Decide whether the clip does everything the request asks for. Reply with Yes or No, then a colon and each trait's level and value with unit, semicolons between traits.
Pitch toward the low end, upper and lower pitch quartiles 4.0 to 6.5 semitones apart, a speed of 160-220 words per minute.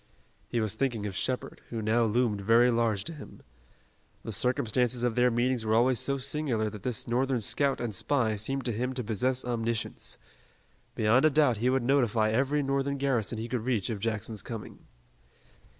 No: low, 120 Hz; average, 2.9 semitones; average, 180 wpm